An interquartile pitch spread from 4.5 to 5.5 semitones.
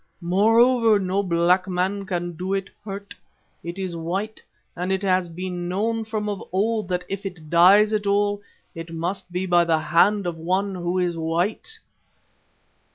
No: narrow, 2.6 semitones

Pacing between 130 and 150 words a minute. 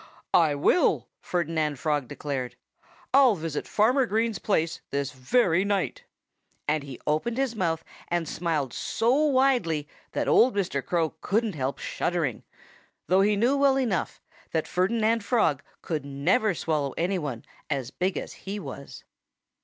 Yes: average, 140 wpm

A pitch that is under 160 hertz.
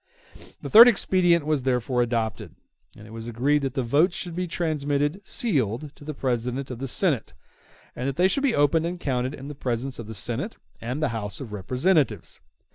Yes: low, 135 Hz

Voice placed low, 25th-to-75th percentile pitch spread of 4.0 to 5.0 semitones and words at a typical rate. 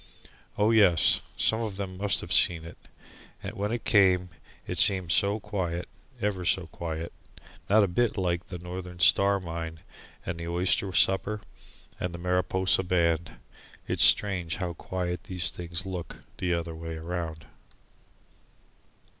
No: very low, 90 Hz; narrow, 2.5 semitones; average, 155 wpm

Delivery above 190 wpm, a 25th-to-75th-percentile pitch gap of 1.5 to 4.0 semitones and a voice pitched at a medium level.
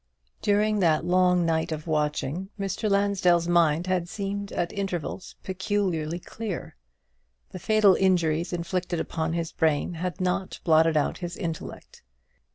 No: slow, 135 wpm; average, 3.0 semitones; medium, 175 Hz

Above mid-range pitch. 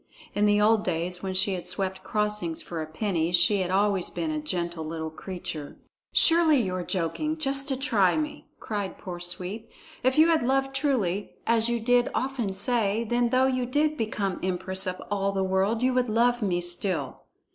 Yes: high, 205 Hz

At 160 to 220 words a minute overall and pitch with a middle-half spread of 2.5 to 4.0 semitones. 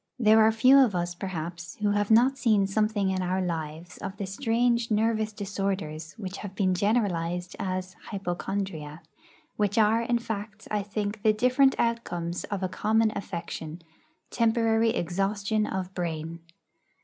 No: average, 150 wpm; average, 3.6 semitones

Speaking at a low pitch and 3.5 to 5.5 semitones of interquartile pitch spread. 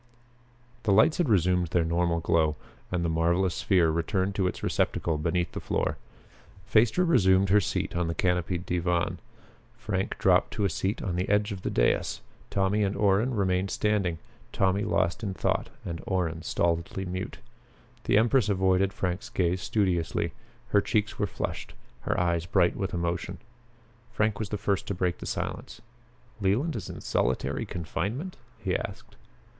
No: very low, 95 Hz; average, 3.0 semitones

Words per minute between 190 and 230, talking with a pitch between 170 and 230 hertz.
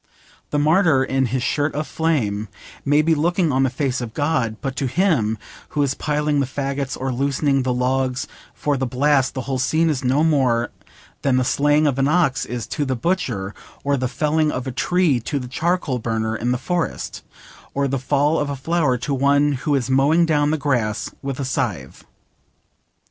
No: average, 195 wpm; low, 135 Hz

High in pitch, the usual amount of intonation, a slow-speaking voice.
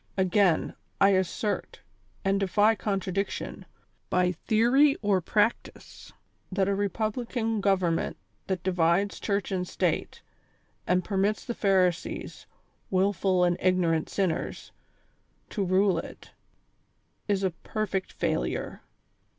No: high, 195 Hz; narrow, 2.0 semitones; slow, 105 wpm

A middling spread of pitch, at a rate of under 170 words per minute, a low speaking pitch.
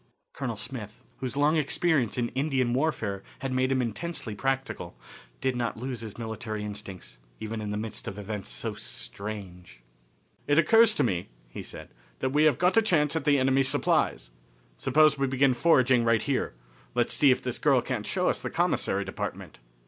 No: average, 5.0 semitones; average, 180 wpm; low, 130 Hz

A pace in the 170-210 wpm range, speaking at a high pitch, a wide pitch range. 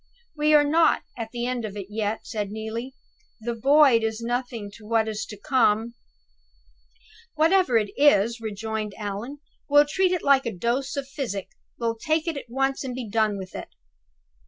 No: average, 180 wpm; high, 235 Hz; average, 4.3 semitones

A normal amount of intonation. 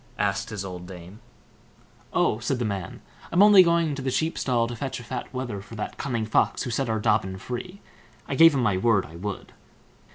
Yes: average, 5.0 semitones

